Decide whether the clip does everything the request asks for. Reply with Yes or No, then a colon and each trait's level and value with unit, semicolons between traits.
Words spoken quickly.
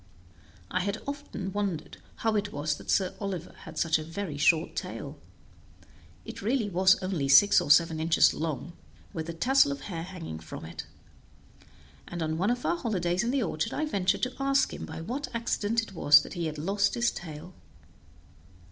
No: average, 185 wpm